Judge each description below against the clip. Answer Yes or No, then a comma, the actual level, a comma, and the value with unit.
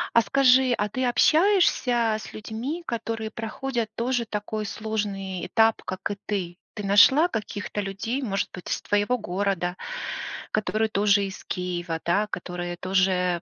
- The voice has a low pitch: No, high, 210 Hz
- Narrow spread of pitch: No, average, 3.3 semitones